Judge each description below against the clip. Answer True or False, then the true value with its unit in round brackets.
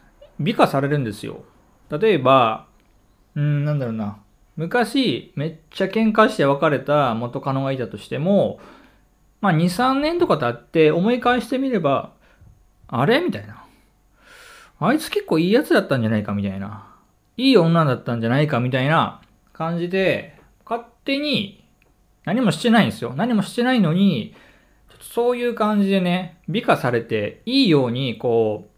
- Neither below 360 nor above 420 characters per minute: False (310 characters per minute)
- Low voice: False (165 Hz)